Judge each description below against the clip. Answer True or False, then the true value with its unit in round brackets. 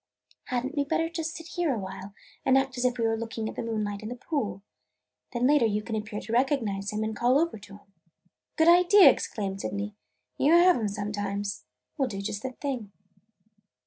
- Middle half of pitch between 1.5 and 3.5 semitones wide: False (5.1 semitones)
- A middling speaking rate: False (210 wpm)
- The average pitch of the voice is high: True (230 Hz)